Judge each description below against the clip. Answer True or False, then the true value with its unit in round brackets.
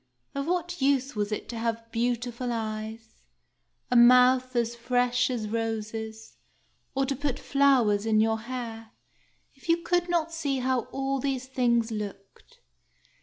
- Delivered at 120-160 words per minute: True (145 wpm)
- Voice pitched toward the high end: True (245 Hz)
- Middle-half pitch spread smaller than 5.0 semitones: True (3.3 semitones)